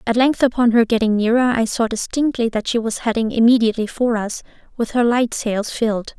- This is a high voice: Yes, high, 230 Hz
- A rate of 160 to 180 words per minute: No, fast, 205 wpm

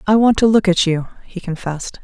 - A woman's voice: Yes, female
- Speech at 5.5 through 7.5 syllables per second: Yes, 5.7 syllables/s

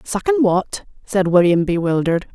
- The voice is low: No, high, 195 Hz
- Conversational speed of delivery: No, slow, 130 wpm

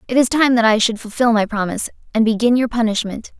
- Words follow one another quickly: Yes, fast, 230 wpm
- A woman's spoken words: Yes, female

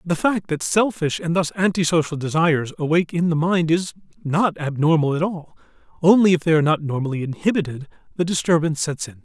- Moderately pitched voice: Yes, medium, 165 Hz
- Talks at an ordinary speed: Yes, average, 180 wpm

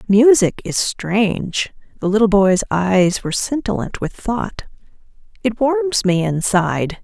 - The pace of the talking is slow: Yes, slow, 130 wpm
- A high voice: Yes, high, 205 Hz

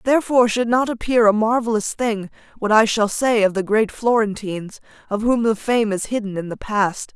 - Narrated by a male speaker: No, female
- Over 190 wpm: Yes, average, 200 wpm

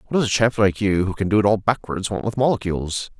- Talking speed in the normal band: No, fast, 280 wpm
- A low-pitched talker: Yes, low, 105 Hz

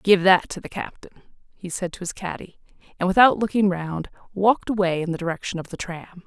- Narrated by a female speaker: Yes, female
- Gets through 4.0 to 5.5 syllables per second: No, 5.9 syllables/s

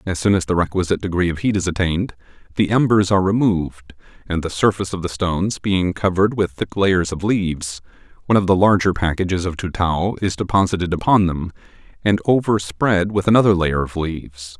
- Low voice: Yes, very low, 95 Hz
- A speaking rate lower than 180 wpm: No, average, 185 wpm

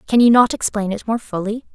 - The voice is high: Yes, high, 220 Hz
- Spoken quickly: Yes, fast, 240 wpm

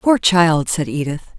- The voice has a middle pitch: Yes, medium, 165 Hz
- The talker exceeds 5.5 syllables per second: No, 4.1 syllables/s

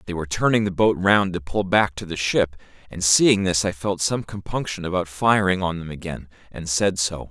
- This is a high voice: No, very low, 90 Hz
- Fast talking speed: Yes, fast, 220 wpm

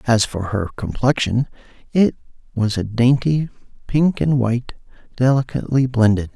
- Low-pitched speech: Yes, low, 125 Hz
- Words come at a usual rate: No, slow, 125 wpm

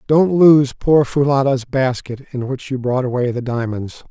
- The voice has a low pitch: Yes, low, 130 Hz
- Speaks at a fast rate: No, average, 175 wpm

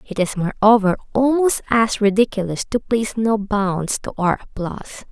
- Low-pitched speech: No, high, 210 Hz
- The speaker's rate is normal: Yes, average, 155 wpm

